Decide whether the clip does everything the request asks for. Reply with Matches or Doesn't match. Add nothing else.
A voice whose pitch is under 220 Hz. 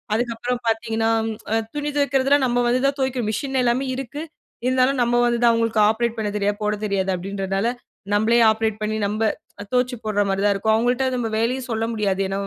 Doesn't match